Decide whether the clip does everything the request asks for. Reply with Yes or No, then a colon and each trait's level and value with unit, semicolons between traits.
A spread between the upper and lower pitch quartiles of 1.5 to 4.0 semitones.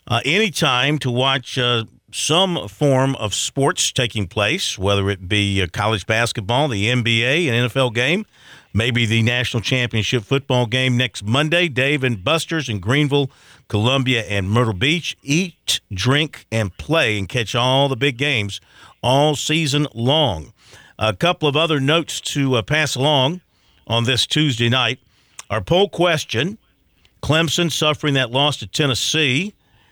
No: average, 5.0 semitones